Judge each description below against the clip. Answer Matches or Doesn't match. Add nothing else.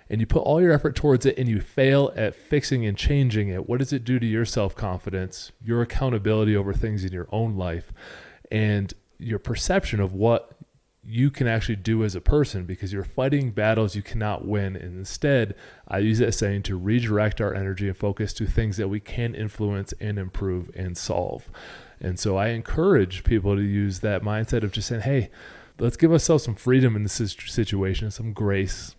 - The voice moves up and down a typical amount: Matches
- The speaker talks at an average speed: Matches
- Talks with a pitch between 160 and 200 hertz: Doesn't match